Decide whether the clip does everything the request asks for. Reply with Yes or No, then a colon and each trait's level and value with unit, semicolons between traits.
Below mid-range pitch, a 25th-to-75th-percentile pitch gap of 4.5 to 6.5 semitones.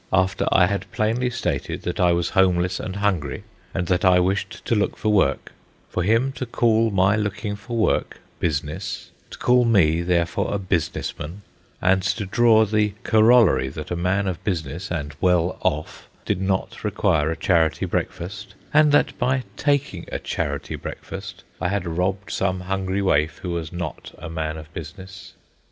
No: very low, 95 Hz; average, 3.4 semitones